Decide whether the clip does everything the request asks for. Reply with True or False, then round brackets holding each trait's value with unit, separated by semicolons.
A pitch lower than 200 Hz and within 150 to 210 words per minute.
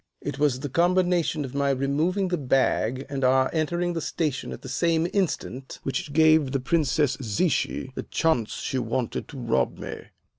True (140 Hz; 175 wpm)